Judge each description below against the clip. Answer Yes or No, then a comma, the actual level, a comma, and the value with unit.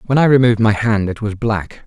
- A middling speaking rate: No, fast, 260 wpm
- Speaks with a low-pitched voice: Yes, low, 110 Hz